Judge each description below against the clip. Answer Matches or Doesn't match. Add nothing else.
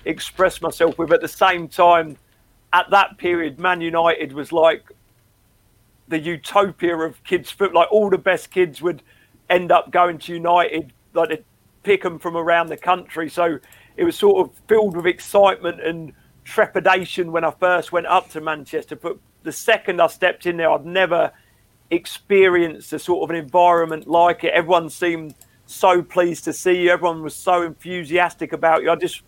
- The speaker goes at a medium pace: Matches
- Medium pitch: Matches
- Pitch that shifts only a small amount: Matches